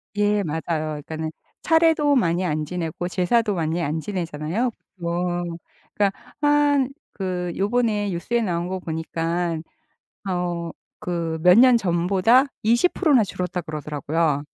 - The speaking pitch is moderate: Yes, medium, 180 Hz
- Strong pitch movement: No, average, 4.4 semitones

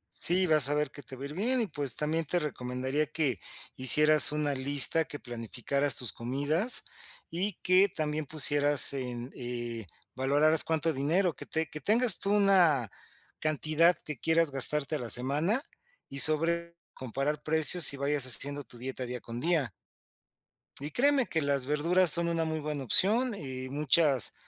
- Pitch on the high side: No, medium, 150 Hz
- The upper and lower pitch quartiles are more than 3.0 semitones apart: Yes, average, 3.7 semitones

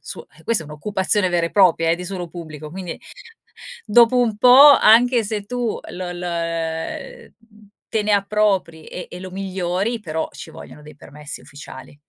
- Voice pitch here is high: No, medium, 180 Hz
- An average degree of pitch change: Yes, average, 4.3 semitones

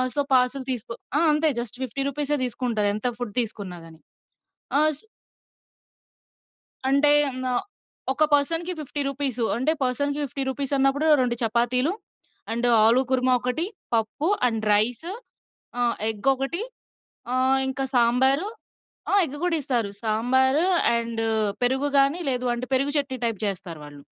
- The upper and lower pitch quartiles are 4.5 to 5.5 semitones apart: No, average, 3.3 semitones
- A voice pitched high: Yes, very high, 255 Hz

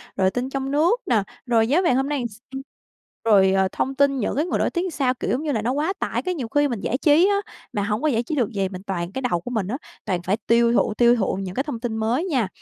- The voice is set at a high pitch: Yes, high, 245 Hz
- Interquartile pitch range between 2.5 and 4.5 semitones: No, average, 5.3 semitones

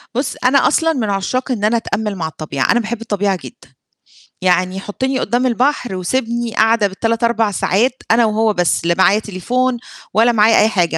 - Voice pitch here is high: Yes, high, 220 Hz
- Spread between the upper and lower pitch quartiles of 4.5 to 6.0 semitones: No, average, 3.8 semitones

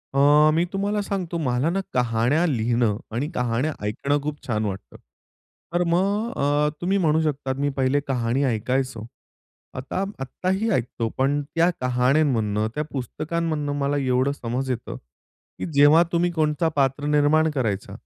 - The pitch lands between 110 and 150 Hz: Yes, medium, 140 Hz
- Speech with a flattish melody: No, average, 4.3 semitones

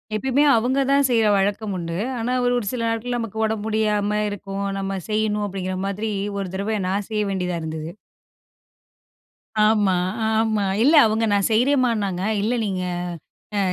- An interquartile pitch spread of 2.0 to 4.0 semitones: Yes, narrow, 2.6 semitones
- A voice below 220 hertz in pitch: Yes, high, 210 Hz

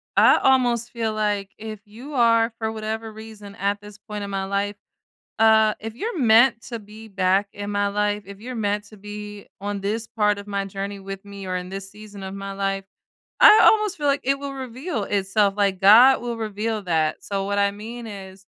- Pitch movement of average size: No, narrow, 2.2 semitones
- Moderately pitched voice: No, high, 210 Hz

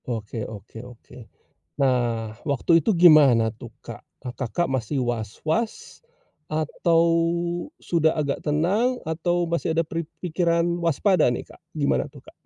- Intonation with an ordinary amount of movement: No, wide, 5.7 semitones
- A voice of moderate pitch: Yes, medium, 155 Hz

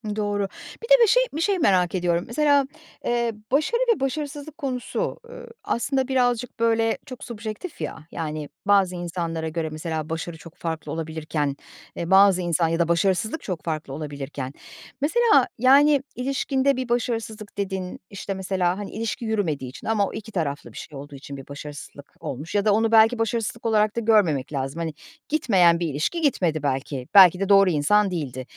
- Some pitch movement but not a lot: No, wide, 6.8 semitones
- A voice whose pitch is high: Yes, high, 195 Hz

